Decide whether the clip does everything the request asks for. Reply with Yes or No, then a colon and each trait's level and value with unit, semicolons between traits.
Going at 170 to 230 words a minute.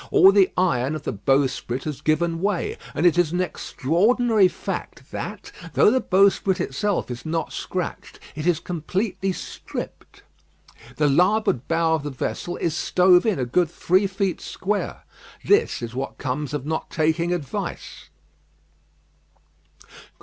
No: average, 145 wpm